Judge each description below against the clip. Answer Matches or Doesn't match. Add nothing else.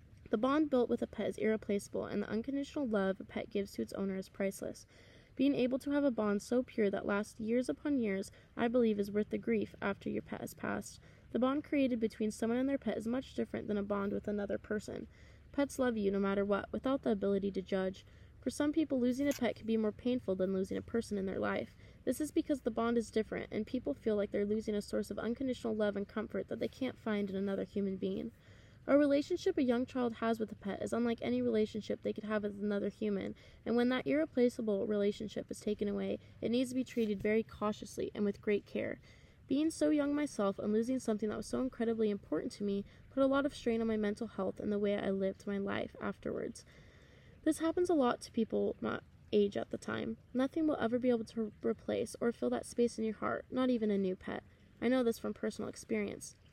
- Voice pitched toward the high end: Matches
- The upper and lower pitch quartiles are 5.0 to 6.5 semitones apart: Doesn't match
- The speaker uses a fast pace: Matches